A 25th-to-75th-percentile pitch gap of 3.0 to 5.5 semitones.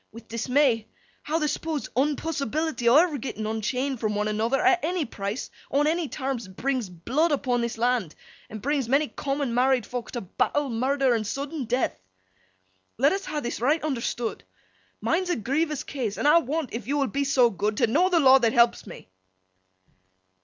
Yes: average, 4.3 semitones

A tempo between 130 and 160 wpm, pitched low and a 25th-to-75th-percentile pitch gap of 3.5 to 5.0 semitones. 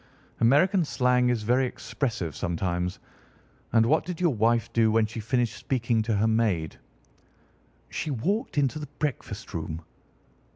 Yes: average, 140 wpm; low, 115 Hz; average, 3.8 semitones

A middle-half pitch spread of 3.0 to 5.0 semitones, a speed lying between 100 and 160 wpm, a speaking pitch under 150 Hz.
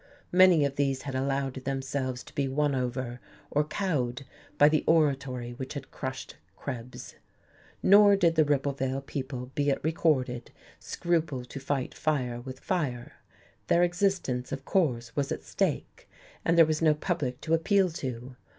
Yes: average, 3.5 semitones; average, 155 wpm; medium, 140 Hz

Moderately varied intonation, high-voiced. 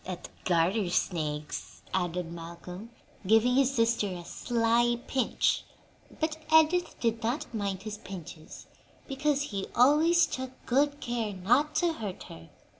No: wide, 6.7 semitones; high, 230 Hz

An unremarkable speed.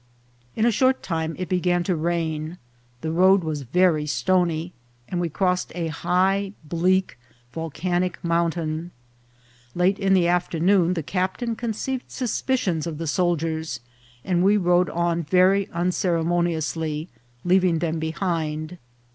No: slow, 130 wpm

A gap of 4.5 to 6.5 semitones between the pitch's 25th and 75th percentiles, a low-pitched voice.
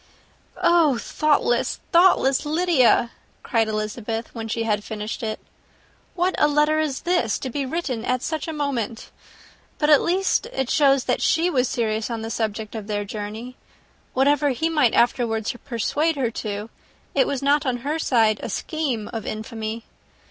No: average, 5.1 semitones; very high, 255 Hz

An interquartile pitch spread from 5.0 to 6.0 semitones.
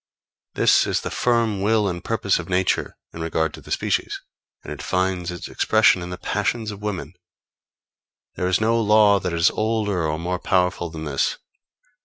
No: average, 3.5 semitones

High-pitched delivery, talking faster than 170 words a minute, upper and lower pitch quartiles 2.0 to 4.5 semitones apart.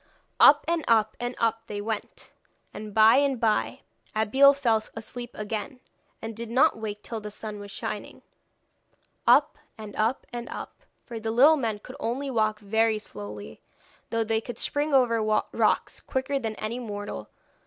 No: high, 225 Hz; average, 165 wpm; narrow, 2.4 semitones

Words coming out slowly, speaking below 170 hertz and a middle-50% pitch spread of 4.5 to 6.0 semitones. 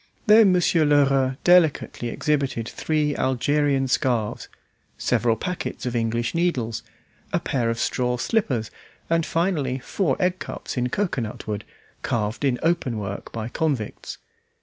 Yes: slow, 125 wpm; low, 135 Hz; wide, 5.6 semitones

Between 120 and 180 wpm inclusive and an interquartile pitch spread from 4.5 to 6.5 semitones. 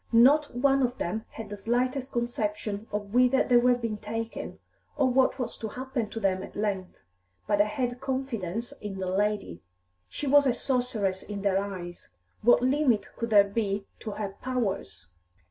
No: average, 175 wpm; average, 3.8 semitones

